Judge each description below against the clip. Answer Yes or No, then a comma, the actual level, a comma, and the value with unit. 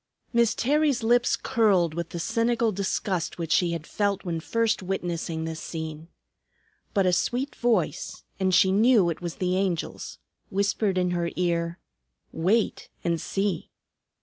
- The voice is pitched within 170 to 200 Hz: Yes, medium, 185 Hz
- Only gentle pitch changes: No, average, 4.6 semitones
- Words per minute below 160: Yes, average, 150 wpm